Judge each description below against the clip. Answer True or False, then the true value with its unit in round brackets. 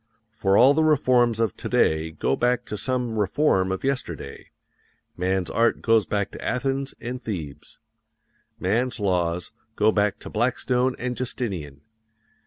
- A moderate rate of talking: True (145 wpm)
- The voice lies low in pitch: True (115 Hz)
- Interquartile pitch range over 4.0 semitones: True (5.1 semitones)